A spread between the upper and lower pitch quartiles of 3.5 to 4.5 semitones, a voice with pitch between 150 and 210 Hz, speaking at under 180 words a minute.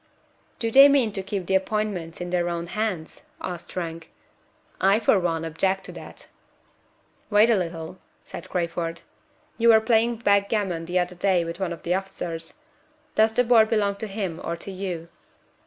Yes: average, 3.9 semitones; high, 190 Hz; average, 170 wpm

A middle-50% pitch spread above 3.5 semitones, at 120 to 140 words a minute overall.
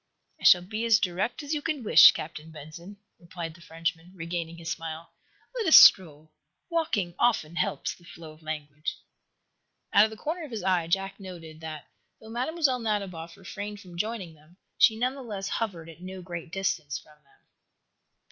No: average, 5.0 semitones; average, 180 wpm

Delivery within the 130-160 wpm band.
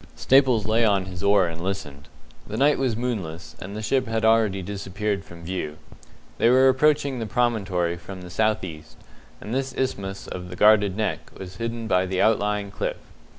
No: average, 185 wpm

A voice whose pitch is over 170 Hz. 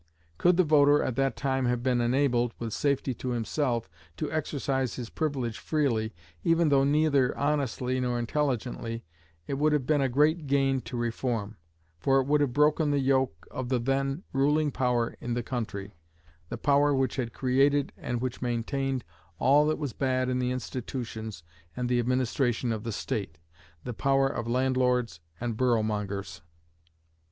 No: low, 130 Hz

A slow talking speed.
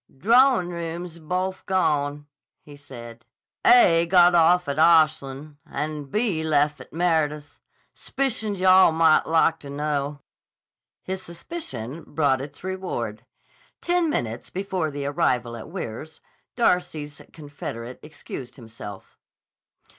Yes: slow, 125 wpm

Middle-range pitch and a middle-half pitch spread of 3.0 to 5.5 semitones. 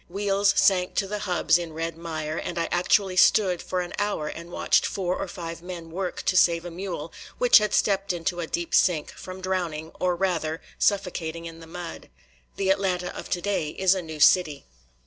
No: medium, 180 Hz; narrow, 2.5 semitones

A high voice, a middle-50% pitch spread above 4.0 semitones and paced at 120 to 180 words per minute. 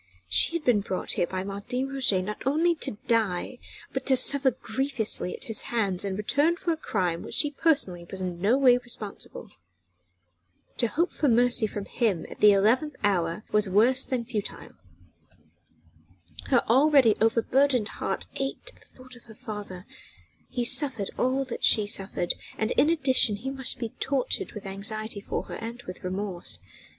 Yes: high, 230 Hz; average, 4.8 semitones; average, 170 wpm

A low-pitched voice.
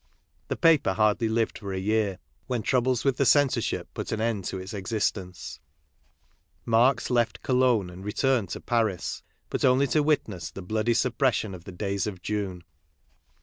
Yes: low, 110 Hz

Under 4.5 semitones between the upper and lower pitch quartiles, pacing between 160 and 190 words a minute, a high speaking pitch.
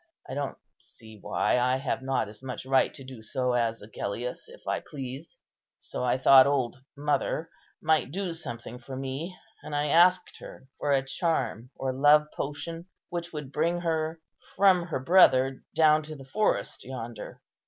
No: average, 3.8 semitones; average, 170 wpm; low, 135 Hz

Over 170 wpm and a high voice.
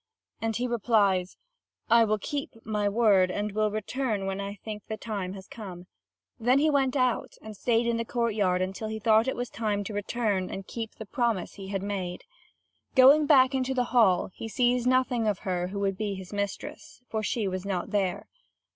Yes: average, 200 wpm; high, 215 Hz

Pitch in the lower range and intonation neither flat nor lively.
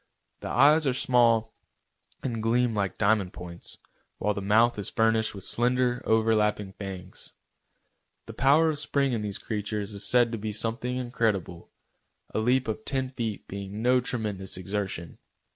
Yes: low, 110 Hz; average, 3.3 semitones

